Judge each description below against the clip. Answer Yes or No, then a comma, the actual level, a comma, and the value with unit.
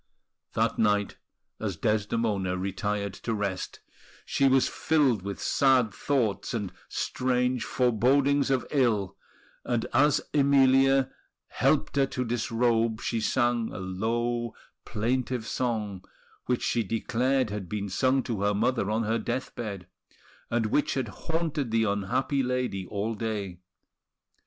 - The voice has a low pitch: Yes, low, 115 Hz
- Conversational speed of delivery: No, slow, 130 wpm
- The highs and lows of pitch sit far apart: No, average, 3.8 semitones